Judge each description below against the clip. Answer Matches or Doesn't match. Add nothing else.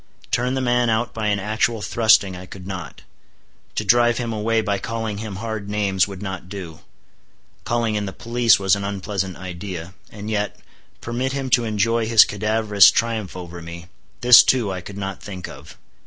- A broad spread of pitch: Doesn't match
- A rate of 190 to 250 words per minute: Doesn't match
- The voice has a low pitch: Matches